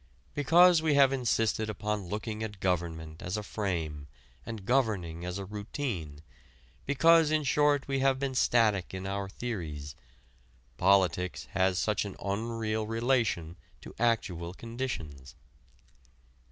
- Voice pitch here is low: Yes, low, 105 Hz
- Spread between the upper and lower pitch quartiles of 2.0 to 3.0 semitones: No, wide, 5.6 semitones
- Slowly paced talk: Yes, slow, 125 wpm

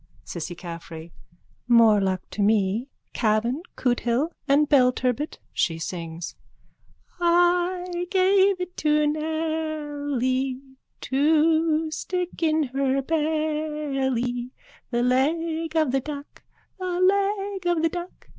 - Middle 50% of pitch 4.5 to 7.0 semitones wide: Yes, average, 5.0 semitones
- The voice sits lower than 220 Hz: No, very high, 300 Hz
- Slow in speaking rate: Yes, slow, 105 wpm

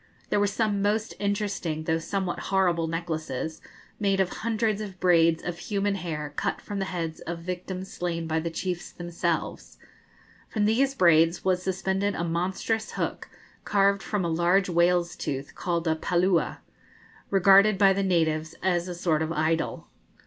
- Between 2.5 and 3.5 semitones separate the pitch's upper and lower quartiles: Yes, average, 3.0 semitones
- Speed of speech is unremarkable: Yes, average, 160 wpm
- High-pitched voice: No, medium, 180 Hz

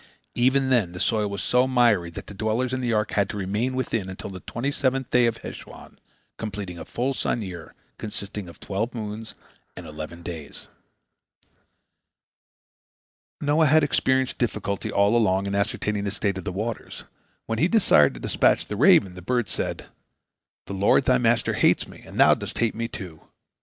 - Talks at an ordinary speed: Yes, average, 180 wpm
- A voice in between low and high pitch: No, low, 105 Hz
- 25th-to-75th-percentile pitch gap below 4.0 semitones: No, average, 4.4 semitones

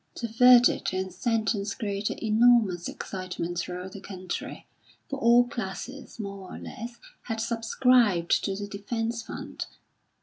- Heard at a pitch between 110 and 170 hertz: No, high, 215 Hz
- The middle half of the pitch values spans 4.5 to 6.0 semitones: No, average, 3.7 semitones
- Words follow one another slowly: Yes, slow, 130 wpm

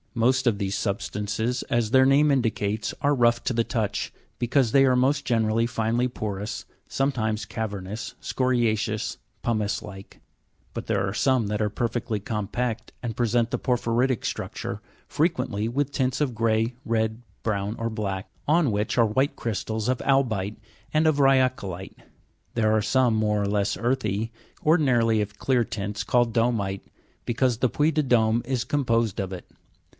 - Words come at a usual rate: Yes, average, 160 wpm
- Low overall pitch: Yes, low, 115 Hz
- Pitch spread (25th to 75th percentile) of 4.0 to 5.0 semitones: No, average, 3.2 semitones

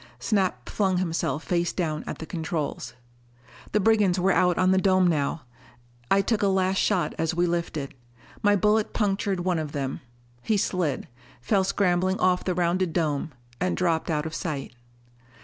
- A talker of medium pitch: Yes, medium, 180 Hz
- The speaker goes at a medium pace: Yes, average, 165 wpm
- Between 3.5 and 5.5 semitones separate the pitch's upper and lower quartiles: No, average, 3.0 semitones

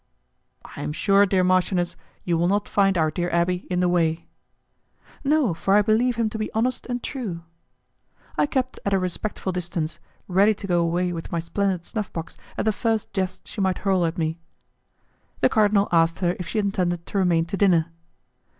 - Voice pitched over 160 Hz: Yes, medium, 185 Hz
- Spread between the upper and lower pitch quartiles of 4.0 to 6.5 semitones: No, average, 3.1 semitones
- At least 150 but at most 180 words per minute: No, average, 195 wpm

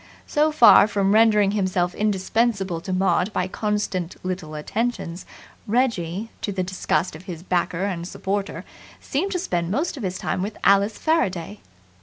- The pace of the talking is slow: No, average, 155 wpm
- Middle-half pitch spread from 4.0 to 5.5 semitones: No, average, 3.3 semitones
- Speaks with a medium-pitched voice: No, high, 195 Hz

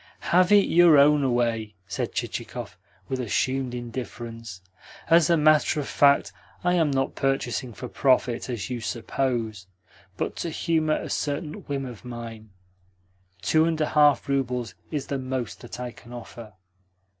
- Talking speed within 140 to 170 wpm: Yes, average, 155 wpm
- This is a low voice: Yes, low, 130 Hz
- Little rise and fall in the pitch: No, average, 4.0 semitones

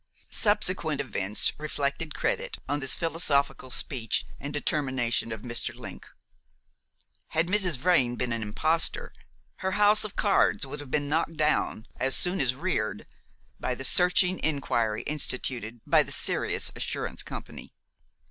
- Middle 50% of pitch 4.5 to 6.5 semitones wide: Yes, average, 5.2 semitones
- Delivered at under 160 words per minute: Yes, average, 140 wpm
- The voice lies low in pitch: No, medium, 145 Hz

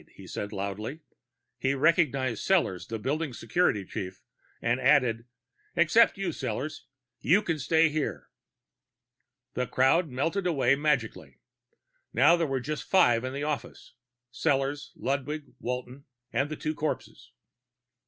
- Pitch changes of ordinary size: Yes, average, 4.1 semitones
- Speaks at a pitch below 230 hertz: Yes, medium, 140 Hz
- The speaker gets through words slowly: Yes, slow, 130 wpm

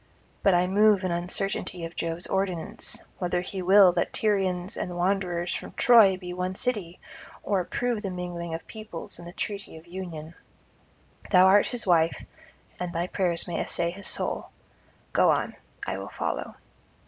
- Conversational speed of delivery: Yes, average, 165 wpm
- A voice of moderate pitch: Yes, medium, 180 Hz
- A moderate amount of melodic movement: No, narrow, 2.2 semitones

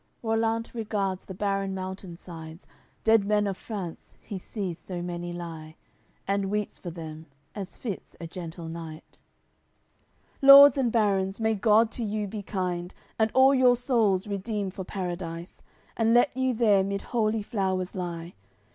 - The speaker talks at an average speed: Yes, average, 160 wpm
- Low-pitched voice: No, high, 195 Hz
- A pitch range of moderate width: Yes, average, 3.9 semitones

